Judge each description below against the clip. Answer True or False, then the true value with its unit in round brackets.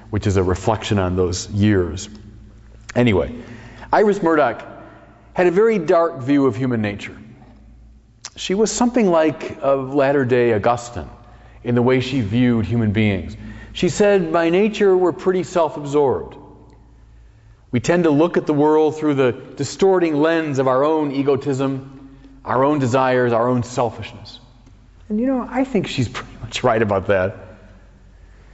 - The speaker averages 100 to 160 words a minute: True (155 wpm)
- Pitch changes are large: True (6.1 semitones)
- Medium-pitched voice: False (130 Hz)